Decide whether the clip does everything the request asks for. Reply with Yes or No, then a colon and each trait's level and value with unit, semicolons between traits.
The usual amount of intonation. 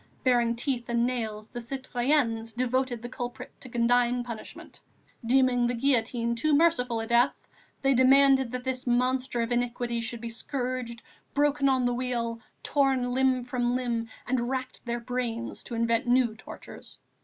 No: narrow, 1.7 semitones